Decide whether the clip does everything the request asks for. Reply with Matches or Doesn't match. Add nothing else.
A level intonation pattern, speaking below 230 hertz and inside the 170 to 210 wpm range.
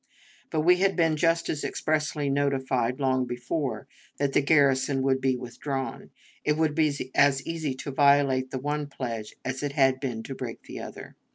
Matches